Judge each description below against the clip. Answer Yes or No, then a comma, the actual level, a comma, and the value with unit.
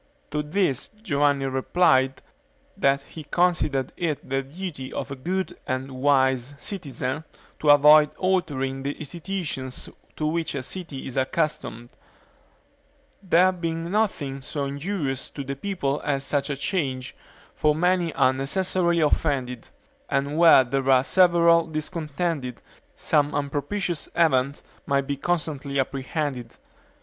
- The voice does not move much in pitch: No, average, 3.9 semitones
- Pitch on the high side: No, medium, 145 Hz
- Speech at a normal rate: No, slow, 125 wpm